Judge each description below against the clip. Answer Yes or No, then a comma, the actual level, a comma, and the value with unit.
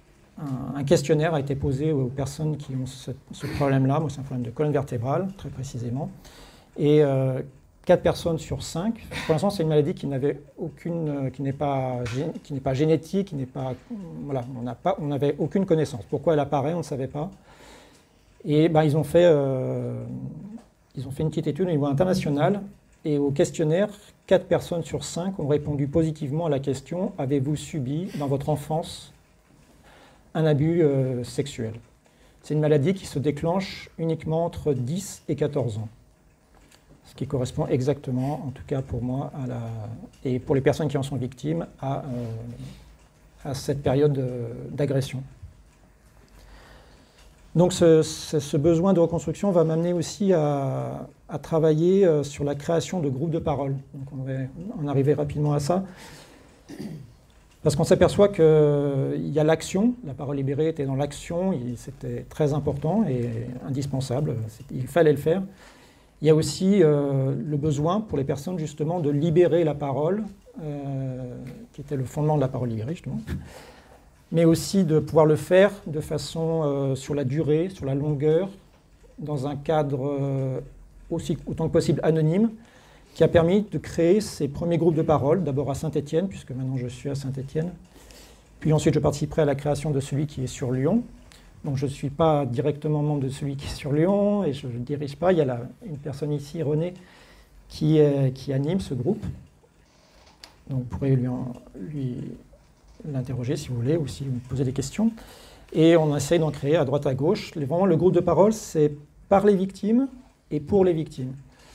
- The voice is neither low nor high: Yes, medium, 150 Hz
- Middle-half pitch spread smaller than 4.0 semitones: Yes, average, 3.4 semitones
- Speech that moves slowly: No, average, 180 wpm